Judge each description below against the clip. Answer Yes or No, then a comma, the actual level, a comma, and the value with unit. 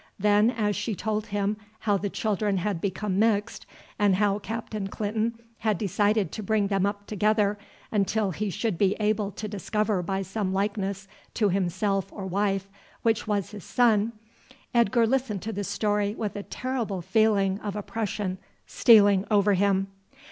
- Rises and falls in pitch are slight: Yes, narrow, 1.7 semitones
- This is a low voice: No, high, 205 Hz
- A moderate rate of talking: Yes, average, 160 wpm